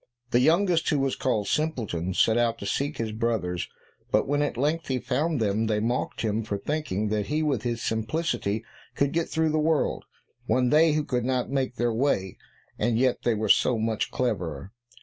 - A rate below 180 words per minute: No, average, 190 wpm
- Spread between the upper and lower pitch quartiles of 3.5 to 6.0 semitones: Yes, average, 5.2 semitones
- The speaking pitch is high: No, low, 120 Hz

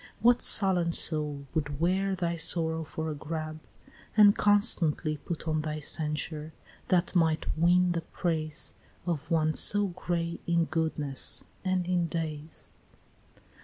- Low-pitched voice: No, medium, 165 Hz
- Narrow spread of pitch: Yes, narrow, 2.3 semitones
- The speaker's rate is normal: No, slow, 130 wpm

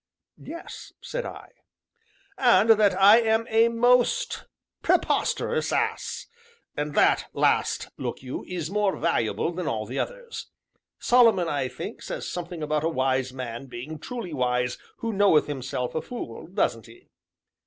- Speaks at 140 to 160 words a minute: Yes, average, 145 wpm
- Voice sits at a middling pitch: Yes, medium, 170 Hz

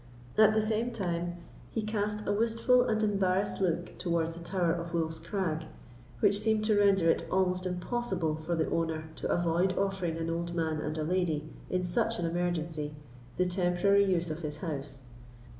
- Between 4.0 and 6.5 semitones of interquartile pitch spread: No, average, 3.5 semitones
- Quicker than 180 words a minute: No, average, 175 wpm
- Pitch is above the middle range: No, medium, 175 Hz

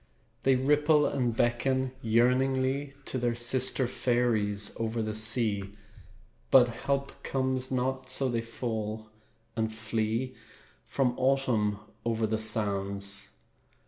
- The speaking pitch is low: Yes, low, 120 Hz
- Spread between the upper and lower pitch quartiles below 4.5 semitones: Yes, average, 3.1 semitones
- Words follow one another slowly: Yes, slow, 110 wpm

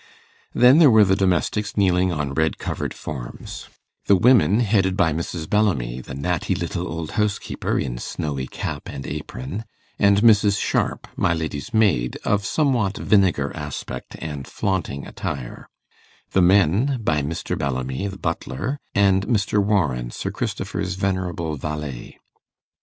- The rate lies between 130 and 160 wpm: Yes, average, 140 wpm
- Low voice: Yes, very low, 90 Hz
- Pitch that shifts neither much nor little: No, wide, 5.8 semitones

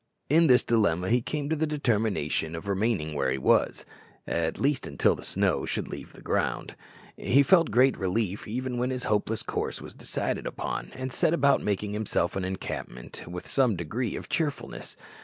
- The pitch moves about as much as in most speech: No, wide, 6.3 semitones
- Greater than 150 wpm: Yes, average, 180 wpm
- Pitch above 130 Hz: No, low, 110 Hz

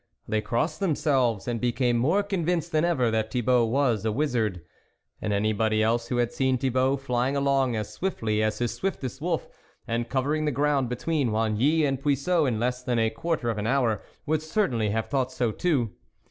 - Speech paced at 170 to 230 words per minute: Yes, average, 190 wpm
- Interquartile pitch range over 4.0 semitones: Yes, average, 4.4 semitones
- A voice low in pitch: Yes, low, 125 Hz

